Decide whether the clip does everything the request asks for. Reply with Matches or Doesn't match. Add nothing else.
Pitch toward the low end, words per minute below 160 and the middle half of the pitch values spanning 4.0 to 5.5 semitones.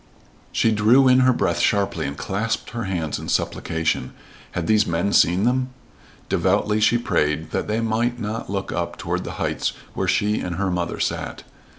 Doesn't match